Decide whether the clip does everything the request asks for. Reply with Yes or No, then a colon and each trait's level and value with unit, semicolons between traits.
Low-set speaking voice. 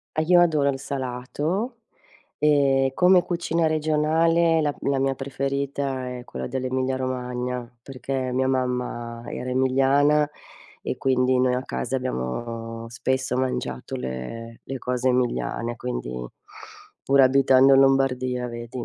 Yes: low, 130 Hz